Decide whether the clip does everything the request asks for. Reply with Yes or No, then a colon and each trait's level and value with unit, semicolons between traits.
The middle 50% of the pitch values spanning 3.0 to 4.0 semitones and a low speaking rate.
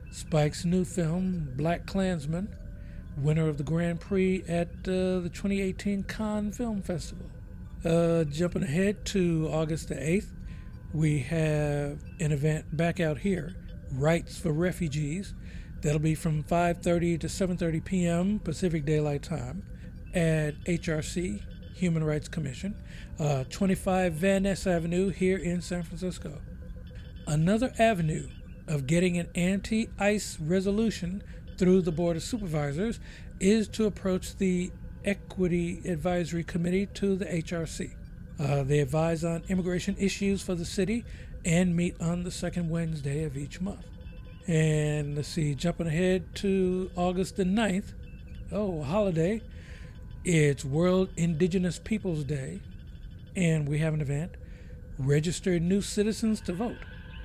Yes: average, 3.4 semitones; slow, 130 wpm